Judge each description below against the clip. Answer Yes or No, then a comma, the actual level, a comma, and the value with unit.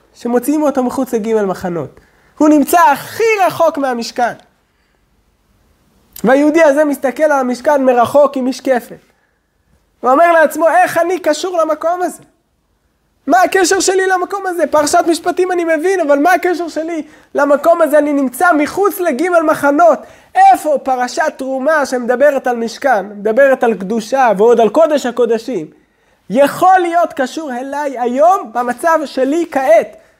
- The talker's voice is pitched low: No, very high, 300 Hz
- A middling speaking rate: Yes, average, 135 wpm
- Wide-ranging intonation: No, average, 4.7 semitones